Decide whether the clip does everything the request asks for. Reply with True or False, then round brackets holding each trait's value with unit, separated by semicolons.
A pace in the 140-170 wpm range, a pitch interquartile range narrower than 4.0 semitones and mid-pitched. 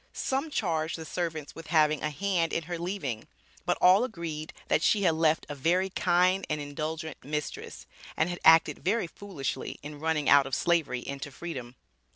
False (180 wpm; 3.0 semitones; 160 Hz)